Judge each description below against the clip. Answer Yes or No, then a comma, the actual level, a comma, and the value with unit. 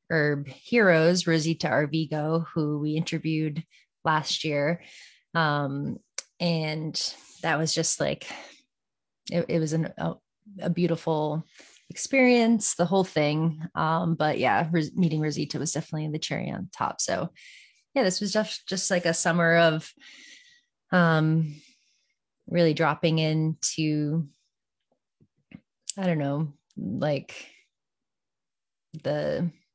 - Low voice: No, medium, 165 Hz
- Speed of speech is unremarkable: No, slow, 115 wpm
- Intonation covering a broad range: No, average, 2.8 semitones